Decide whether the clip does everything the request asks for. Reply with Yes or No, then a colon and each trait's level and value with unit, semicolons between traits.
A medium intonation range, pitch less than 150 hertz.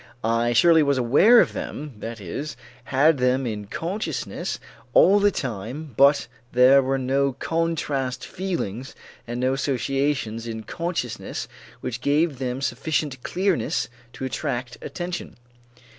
Yes: average, 4.0 semitones; low, 135 Hz